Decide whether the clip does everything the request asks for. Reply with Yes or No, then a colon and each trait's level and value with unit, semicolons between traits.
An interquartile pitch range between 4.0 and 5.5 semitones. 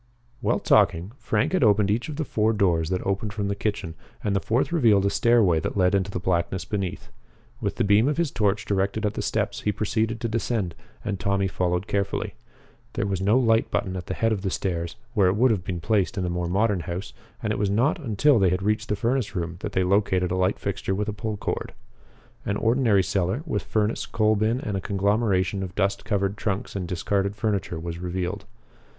No: average, 2.8 semitones